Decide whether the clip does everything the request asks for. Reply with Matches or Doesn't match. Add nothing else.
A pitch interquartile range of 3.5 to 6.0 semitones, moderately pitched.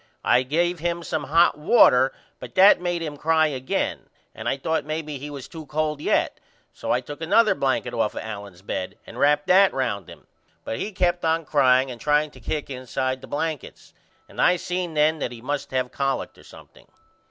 Matches